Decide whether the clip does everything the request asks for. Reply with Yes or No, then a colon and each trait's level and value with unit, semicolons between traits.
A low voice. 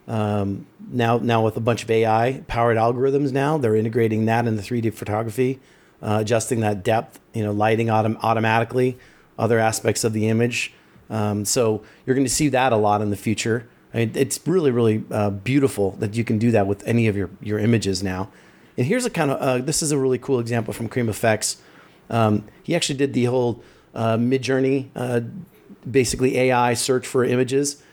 Yes: low, 115 Hz